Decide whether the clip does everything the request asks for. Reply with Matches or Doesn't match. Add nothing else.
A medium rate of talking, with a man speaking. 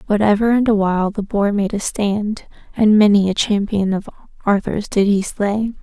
Doesn't match